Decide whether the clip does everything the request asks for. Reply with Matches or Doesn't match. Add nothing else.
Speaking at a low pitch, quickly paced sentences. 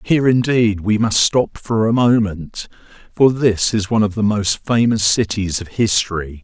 Doesn't match